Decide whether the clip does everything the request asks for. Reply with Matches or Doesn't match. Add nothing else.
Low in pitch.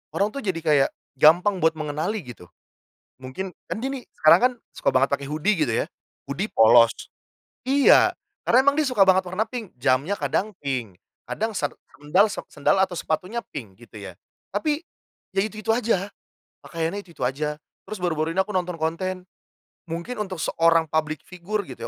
Doesn't match